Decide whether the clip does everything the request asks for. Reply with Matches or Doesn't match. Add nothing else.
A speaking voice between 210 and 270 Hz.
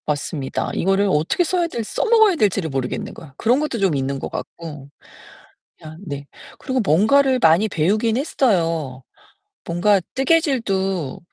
Doesn't match